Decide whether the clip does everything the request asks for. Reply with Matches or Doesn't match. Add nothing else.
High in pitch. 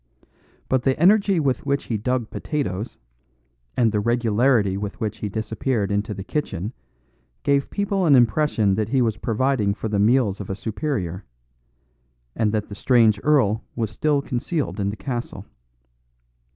Doesn't match